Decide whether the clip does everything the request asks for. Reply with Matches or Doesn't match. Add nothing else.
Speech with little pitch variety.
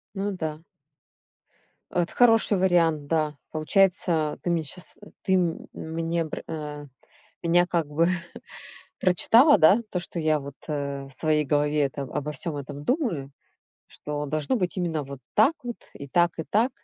Doesn't match